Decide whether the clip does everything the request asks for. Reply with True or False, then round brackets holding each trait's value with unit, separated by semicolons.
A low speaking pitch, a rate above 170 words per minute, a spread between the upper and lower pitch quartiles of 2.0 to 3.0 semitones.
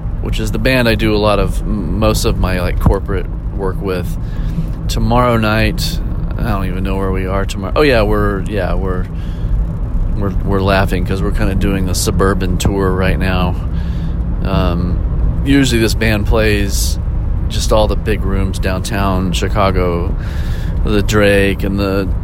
False (95 Hz; 160 wpm; 2.7 semitones)